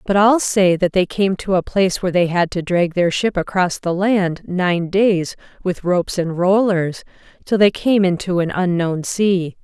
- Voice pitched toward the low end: No, medium, 185 Hz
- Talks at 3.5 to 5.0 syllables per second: Yes, 4.5 syllables/s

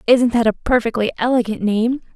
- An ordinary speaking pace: Yes, average, 165 wpm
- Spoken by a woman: Yes, female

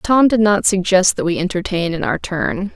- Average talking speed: No, fast, 220 wpm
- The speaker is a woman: Yes, female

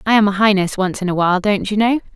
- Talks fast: Yes, fast, 305 wpm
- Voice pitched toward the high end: Yes, high, 200 Hz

